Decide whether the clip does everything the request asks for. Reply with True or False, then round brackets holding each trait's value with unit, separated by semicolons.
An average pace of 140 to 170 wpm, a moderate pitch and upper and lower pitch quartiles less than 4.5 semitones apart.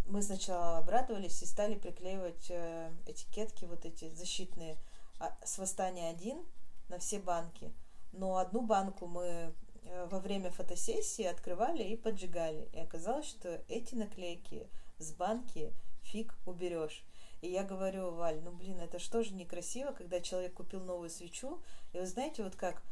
True (145 wpm; 180 Hz; 2.9 semitones)